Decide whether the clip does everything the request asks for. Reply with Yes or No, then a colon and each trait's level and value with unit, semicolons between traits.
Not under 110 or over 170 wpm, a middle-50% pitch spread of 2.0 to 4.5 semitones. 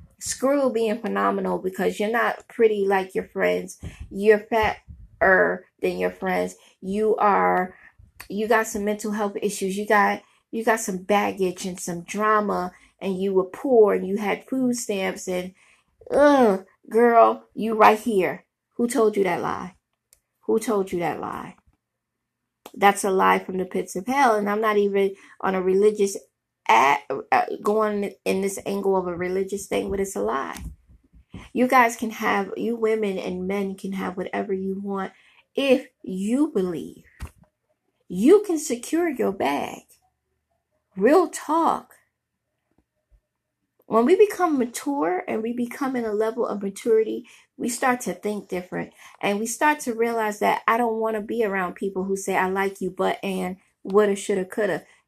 Yes: average, 160 wpm; average, 3.4 semitones